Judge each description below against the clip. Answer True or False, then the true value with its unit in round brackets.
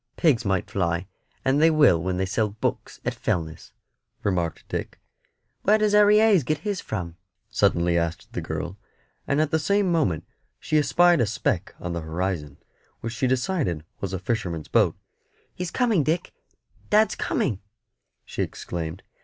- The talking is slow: False (160 wpm)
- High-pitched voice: False (110 Hz)